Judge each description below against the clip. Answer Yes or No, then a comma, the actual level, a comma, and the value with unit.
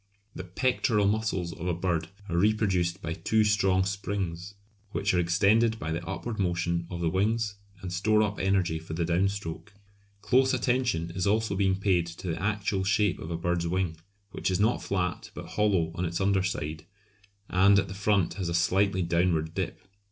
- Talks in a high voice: No, very low, 95 Hz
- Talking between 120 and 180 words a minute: No, average, 190 wpm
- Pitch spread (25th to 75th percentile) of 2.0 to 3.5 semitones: Yes, average, 3.0 semitones